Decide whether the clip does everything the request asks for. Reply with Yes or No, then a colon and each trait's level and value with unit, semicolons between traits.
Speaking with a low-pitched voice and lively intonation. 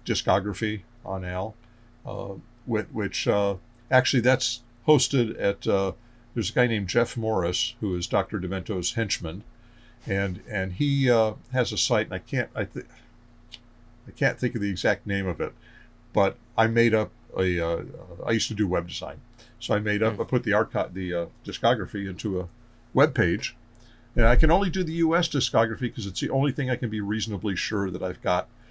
No: low, 115 Hz; average, 3.4 semitones